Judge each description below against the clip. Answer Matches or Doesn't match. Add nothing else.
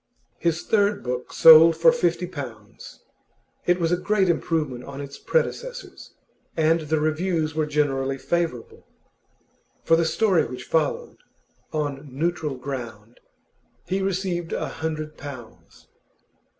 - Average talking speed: Doesn't match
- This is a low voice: Doesn't match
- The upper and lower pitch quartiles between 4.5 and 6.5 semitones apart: Doesn't match